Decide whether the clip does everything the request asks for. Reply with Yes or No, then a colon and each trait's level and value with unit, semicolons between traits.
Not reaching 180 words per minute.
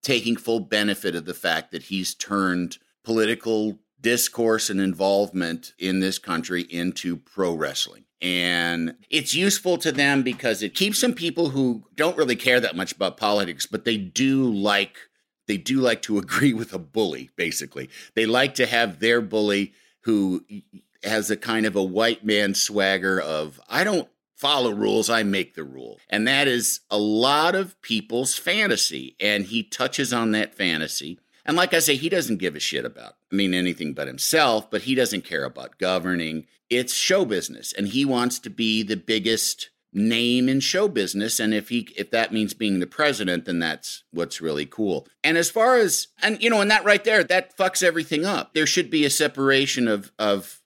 No: average, 190 wpm